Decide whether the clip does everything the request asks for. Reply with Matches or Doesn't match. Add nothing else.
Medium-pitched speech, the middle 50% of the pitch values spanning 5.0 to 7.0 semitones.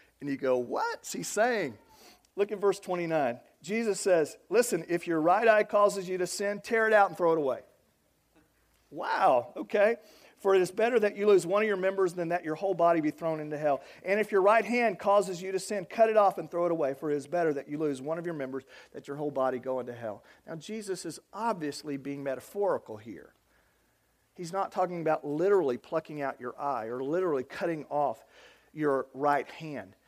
Matches